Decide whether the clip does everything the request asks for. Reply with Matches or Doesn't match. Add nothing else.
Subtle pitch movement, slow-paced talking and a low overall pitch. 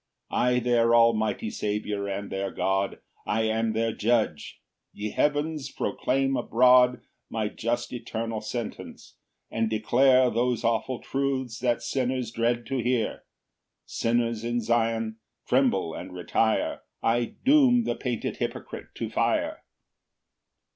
Matches